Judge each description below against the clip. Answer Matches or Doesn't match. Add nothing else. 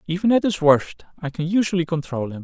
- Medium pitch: Matches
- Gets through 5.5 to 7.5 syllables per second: Matches